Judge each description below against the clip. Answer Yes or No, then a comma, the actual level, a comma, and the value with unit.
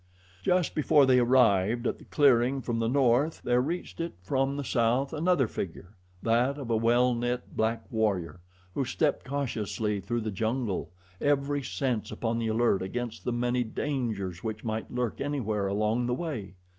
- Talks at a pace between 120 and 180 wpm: Yes, average, 170 wpm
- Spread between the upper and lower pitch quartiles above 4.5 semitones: No, average, 3.7 semitones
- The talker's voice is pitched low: Yes, low, 120 Hz